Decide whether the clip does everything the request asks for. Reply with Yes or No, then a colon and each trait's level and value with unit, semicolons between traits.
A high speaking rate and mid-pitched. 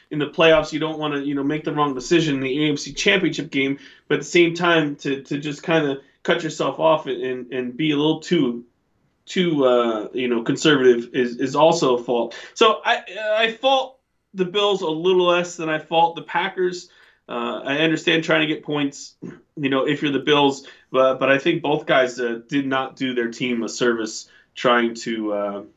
Yes: fast, 210 wpm; medium, 145 Hz